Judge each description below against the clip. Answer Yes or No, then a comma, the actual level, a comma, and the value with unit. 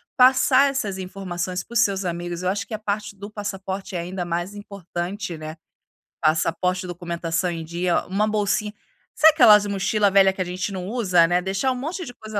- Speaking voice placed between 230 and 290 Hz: No, high, 190 Hz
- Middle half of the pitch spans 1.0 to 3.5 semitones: Yes, average, 2.9 semitones